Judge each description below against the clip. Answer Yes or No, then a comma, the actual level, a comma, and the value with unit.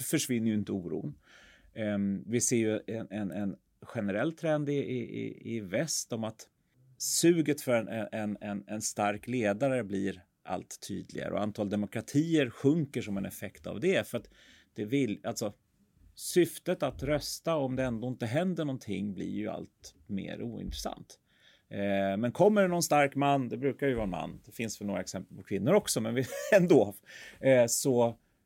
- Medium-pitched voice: No, low, 115 Hz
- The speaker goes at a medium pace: Yes, average, 170 wpm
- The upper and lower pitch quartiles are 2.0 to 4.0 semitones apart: No, wide, 5.4 semitones